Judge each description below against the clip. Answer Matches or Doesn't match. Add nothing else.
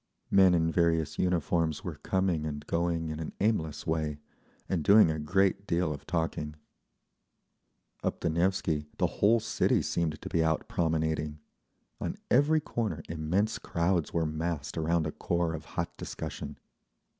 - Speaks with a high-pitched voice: Doesn't match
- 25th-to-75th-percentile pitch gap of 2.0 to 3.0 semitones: Matches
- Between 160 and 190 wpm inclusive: Doesn't match